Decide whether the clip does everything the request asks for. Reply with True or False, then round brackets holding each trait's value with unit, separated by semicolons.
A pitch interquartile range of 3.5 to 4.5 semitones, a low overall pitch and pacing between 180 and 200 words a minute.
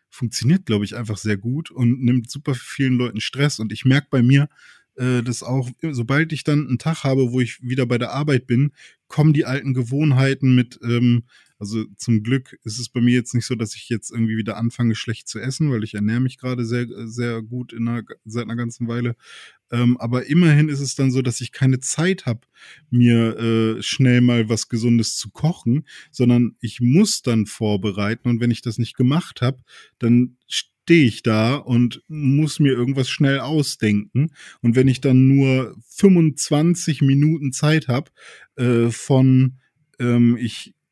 False (2.7 semitones; 125 Hz; 185 wpm)